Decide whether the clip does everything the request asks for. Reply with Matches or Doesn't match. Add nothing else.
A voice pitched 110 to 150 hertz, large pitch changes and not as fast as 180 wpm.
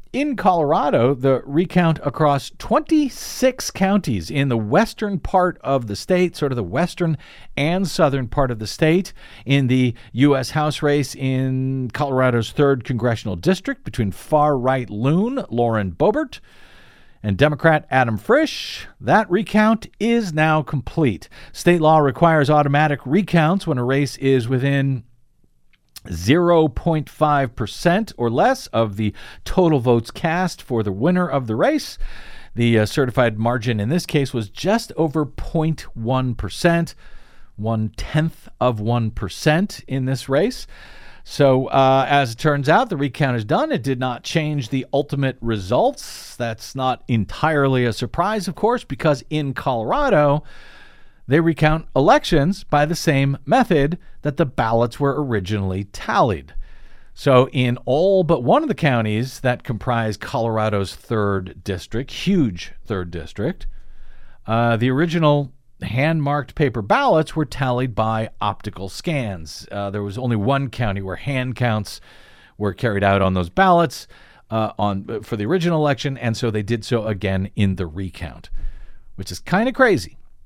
Matches